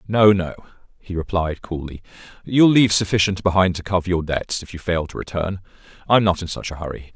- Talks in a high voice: No, very low, 90 Hz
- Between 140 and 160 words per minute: No, average, 200 wpm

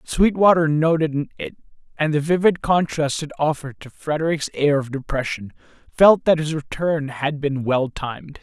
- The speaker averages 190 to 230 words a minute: No, average, 155 wpm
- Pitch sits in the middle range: Yes, medium, 150 Hz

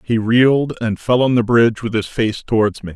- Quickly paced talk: Yes, fast, 245 wpm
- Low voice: Yes, low, 115 Hz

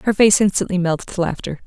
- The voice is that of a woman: Yes, female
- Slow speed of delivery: No, fast, 215 wpm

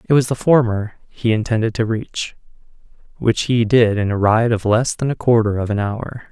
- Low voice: Yes, low, 115 Hz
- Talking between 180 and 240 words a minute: Yes, average, 200 wpm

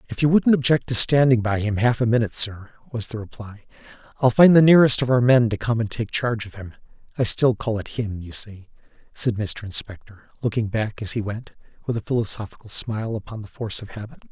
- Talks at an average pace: No, fast, 220 wpm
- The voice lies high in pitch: No, low, 115 Hz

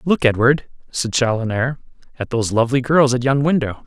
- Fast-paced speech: No, average, 170 wpm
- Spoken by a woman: No, male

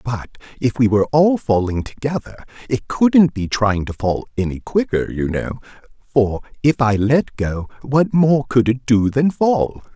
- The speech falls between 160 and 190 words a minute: Yes, average, 175 wpm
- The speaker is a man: Yes, male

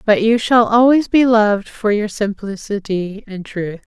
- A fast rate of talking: No, average, 165 wpm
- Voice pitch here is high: Yes, high, 215 Hz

